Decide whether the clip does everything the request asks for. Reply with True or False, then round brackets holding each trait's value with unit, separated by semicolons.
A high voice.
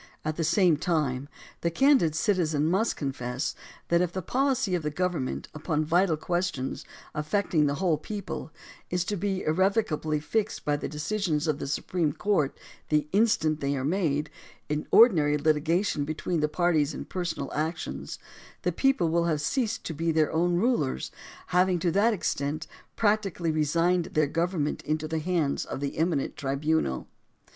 False (160 Hz)